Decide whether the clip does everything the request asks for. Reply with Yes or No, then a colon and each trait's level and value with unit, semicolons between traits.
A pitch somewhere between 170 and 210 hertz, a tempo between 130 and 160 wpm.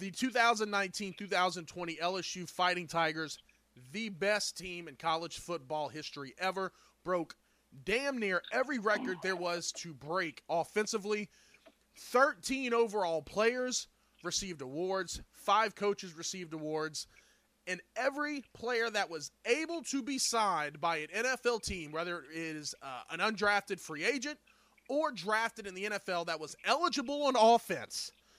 Yes: high, 190 Hz; slow, 135 wpm